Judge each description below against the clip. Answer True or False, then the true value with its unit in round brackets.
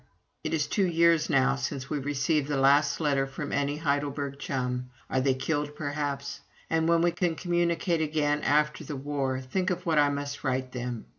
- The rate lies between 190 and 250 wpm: True (195 wpm)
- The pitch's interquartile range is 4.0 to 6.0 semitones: False (2.7 semitones)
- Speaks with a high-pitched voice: False (145 Hz)